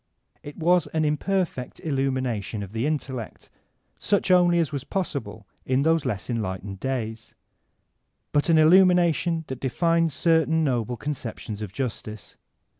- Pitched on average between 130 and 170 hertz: Yes, medium, 140 Hz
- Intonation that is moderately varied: No, wide, 6.2 semitones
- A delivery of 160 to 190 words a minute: No, average, 140 wpm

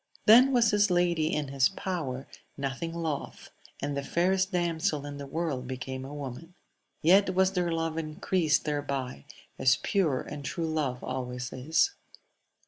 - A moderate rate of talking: Yes, average, 150 wpm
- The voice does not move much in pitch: No, average, 4.4 semitones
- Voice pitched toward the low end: No, medium, 155 Hz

